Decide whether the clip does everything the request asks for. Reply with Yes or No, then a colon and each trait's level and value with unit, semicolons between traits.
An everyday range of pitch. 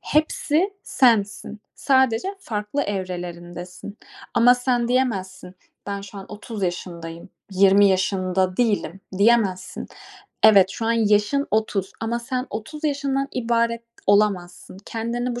Yes: average, 4.3 semitones